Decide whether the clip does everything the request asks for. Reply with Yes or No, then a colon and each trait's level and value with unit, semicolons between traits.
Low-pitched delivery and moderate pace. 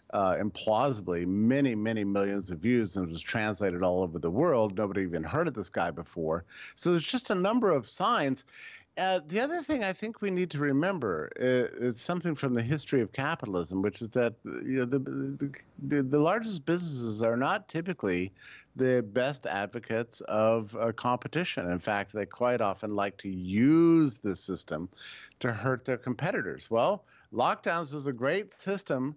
Yes: low, 125 Hz; average, 175 wpm